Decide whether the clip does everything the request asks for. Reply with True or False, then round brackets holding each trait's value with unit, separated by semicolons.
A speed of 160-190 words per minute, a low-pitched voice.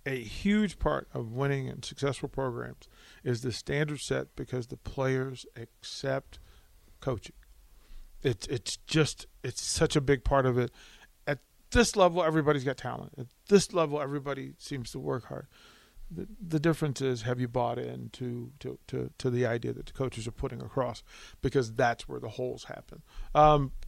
True (170 wpm; 130 Hz)